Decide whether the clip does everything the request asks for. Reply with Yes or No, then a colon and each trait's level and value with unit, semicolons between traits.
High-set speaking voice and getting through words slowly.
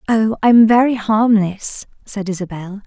Yes: high, 210 Hz; slow, 125 wpm